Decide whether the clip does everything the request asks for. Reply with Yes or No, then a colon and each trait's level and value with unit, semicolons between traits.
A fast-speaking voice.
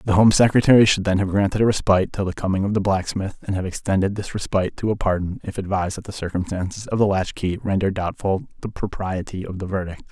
Yes: fast, 230 wpm